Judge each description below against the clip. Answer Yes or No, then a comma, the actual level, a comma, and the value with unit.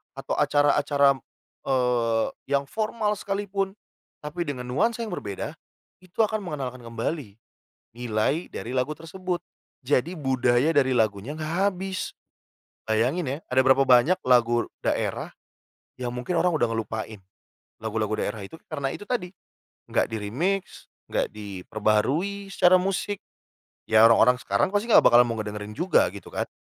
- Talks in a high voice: No, low, 135 Hz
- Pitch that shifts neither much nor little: No, wide, 7.7 semitones